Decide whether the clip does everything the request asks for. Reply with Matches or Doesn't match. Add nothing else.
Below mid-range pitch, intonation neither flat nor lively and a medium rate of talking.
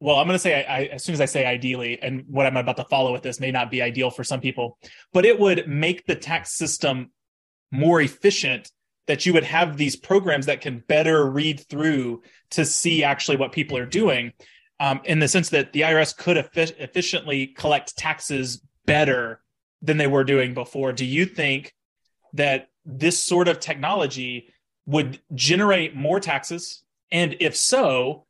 Doesn't match